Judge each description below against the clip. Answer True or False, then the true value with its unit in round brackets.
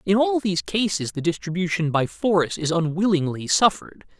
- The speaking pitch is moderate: True (180 Hz)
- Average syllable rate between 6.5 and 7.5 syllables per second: False (5.5 syllables/s)